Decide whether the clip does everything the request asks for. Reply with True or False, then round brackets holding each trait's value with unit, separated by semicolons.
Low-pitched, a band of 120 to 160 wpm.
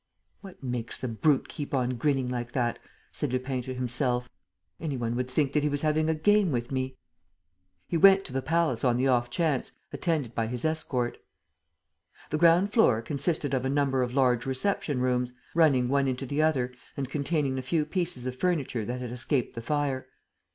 False (130 Hz; 195 wpm)